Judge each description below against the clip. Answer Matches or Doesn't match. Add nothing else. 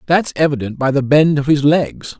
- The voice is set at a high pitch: Doesn't match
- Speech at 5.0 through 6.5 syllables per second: Matches